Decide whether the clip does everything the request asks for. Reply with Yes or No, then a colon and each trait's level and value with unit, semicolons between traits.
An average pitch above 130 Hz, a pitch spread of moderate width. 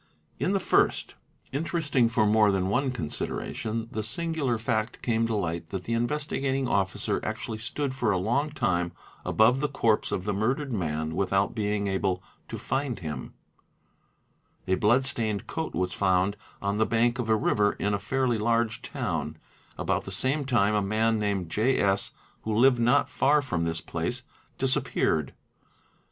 No: low, 110 Hz; average, 4.7 semitones